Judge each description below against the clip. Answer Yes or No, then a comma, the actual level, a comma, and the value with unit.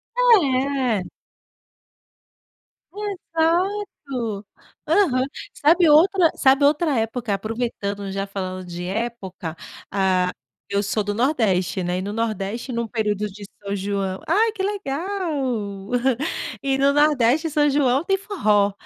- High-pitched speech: Yes, high, 240 Hz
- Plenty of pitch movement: Yes, wide, 7.4 semitones